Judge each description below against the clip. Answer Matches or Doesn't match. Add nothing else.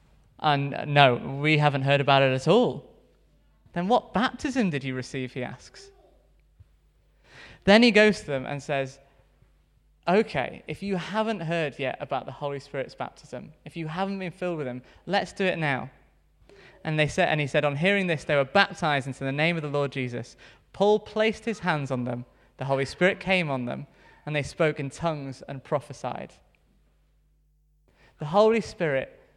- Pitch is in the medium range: Matches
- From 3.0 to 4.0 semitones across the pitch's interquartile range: Doesn't match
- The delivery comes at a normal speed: Matches